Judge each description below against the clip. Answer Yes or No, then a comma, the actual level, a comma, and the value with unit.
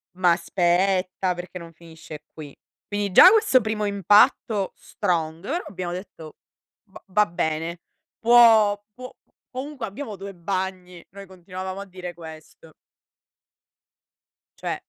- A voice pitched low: No, medium, 185 Hz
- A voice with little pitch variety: No, average, 3.0 semitones